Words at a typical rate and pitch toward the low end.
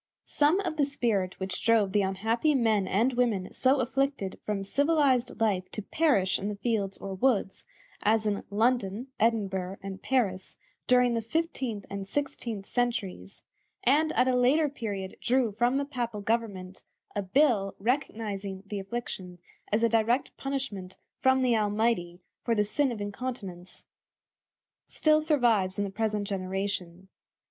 No: average, 150 wpm; high, 220 Hz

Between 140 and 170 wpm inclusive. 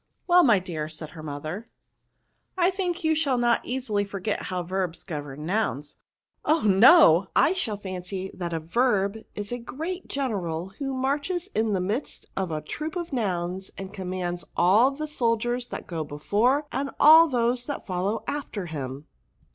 No: average, 180 wpm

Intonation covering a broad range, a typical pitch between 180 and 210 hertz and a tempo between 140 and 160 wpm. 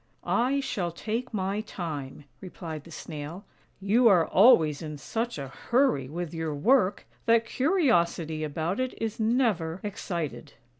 Yes: wide, 6.3 semitones; medium, 185 Hz; average, 155 wpm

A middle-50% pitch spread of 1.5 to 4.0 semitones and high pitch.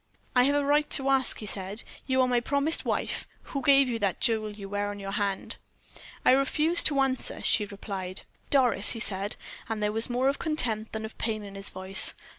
No: average, 5.0 semitones; high, 225 Hz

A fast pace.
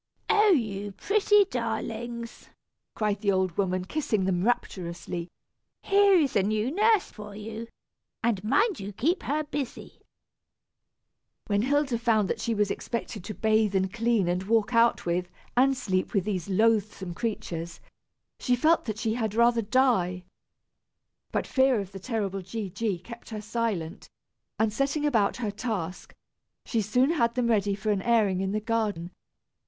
No: average, 160 wpm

